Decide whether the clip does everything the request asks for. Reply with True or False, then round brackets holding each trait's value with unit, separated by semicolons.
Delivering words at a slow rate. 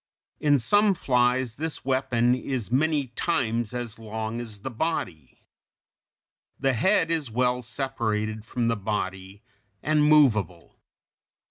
True (120 wpm)